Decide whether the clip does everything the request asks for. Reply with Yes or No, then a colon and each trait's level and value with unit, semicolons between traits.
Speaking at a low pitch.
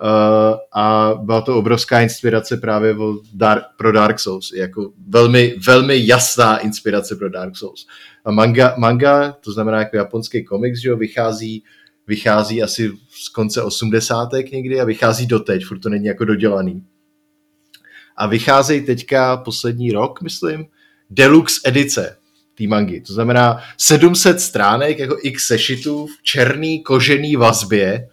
Yes: low, 115 Hz